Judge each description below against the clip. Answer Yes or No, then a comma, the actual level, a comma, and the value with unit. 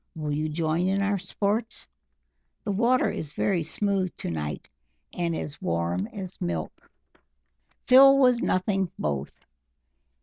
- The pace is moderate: No, slow, 130 wpm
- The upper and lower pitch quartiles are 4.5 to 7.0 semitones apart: Yes, wide, 5.5 semitones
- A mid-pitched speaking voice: Yes, medium, 180 Hz